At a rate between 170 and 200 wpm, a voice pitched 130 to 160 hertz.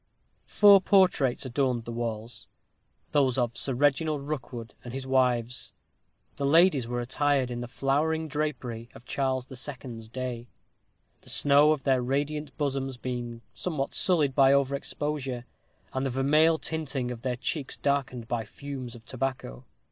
No: average, 155 wpm; low, 135 Hz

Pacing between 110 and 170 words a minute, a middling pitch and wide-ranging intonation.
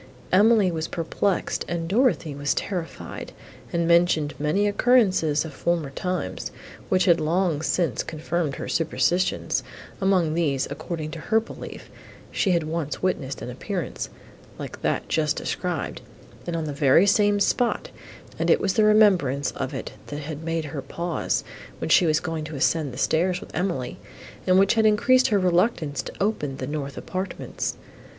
No: average, 160 wpm; medium, 170 Hz; average, 4.0 semitones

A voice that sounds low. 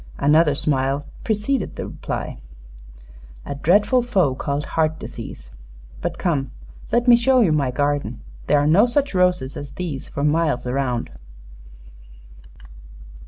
No: medium, 150 Hz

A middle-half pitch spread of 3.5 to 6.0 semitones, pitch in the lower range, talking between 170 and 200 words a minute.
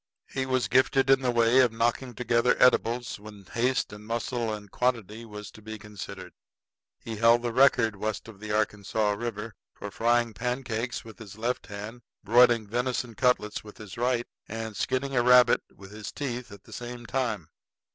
No: narrow, 2.6 semitones; low, 115 Hz; average, 175 wpm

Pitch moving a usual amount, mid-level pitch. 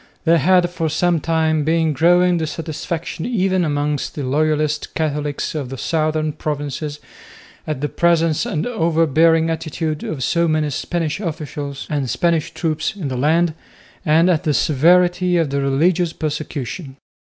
No: narrow, 2.3 semitones; medium, 155 Hz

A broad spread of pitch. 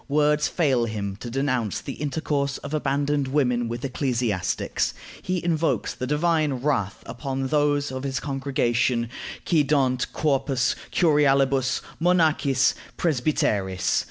No: average, 3.1 semitones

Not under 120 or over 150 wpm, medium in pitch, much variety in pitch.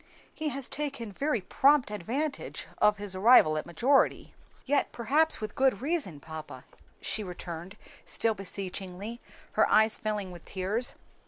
No: average, 145 wpm; high, 215 Hz; wide, 6.4 semitones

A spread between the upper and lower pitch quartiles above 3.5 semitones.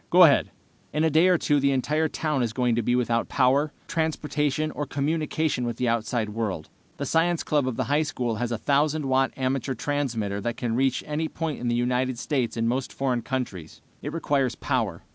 Yes: average, 3.9 semitones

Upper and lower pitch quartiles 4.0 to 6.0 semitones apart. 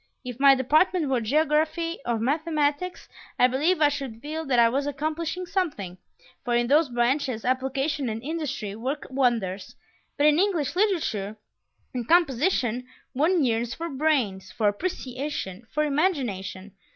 Yes: average, 4.8 semitones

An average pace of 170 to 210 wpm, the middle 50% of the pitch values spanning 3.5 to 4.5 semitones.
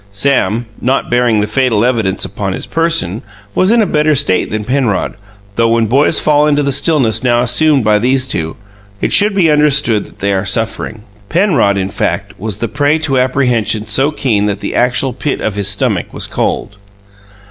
No: average, 190 wpm; wide, 5.4 semitones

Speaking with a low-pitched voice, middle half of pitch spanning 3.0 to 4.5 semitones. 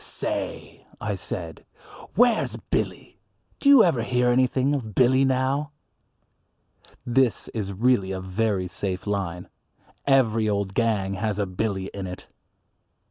No: low, 110 Hz; average, 5.2 semitones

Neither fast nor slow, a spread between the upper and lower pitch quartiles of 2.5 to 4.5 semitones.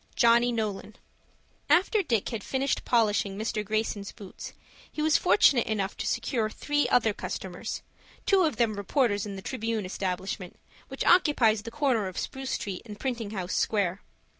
Yes: average, 160 wpm; average, 4.0 semitones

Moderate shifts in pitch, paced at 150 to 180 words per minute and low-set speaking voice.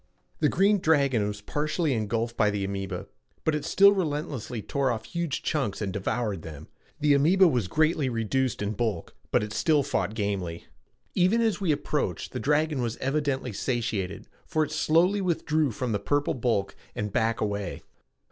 No: wide, 6.8 semitones; average, 170 wpm; low, 130 Hz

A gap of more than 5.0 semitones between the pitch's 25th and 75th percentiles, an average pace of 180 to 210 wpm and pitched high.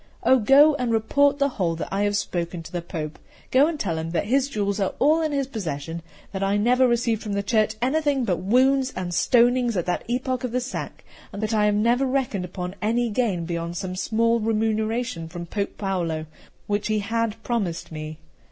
Yes: wide, 5.5 semitones; average, 200 wpm; high, 215 Hz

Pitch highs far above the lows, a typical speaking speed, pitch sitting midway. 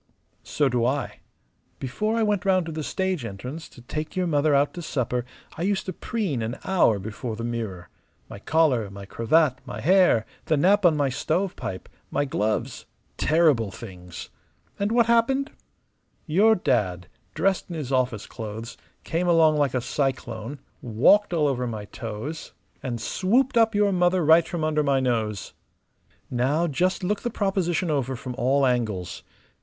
Yes: wide, 7.4 semitones; average, 165 wpm; medium, 145 Hz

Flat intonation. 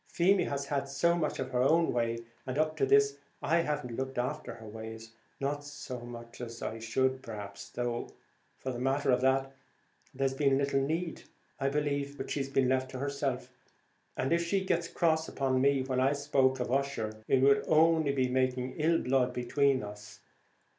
Yes: narrow, 2.3 semitones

